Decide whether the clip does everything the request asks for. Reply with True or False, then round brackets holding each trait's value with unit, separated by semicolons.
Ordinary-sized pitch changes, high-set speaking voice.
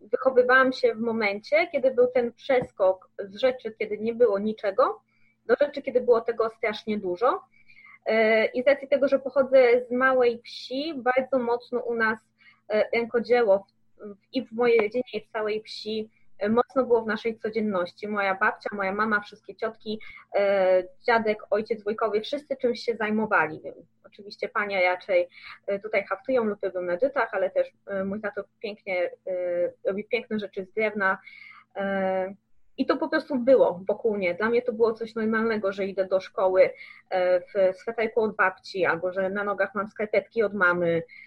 True (3.8 semitones; 220 Hz)